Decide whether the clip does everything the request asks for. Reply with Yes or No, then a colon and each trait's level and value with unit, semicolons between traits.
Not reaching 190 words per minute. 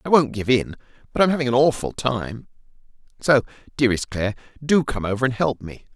No: average, 200 wpm